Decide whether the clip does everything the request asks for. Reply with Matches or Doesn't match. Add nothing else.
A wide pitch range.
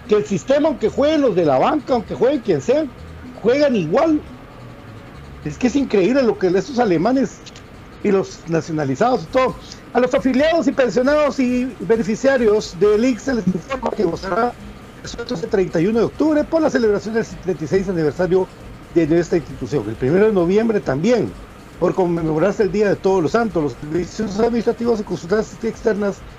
Matches